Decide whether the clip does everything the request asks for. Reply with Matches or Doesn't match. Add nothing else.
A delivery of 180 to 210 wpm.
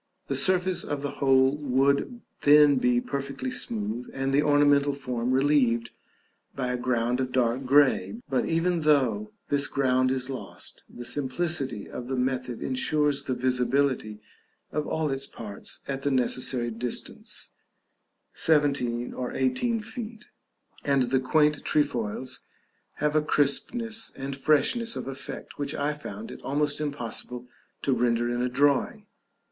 Doesn't match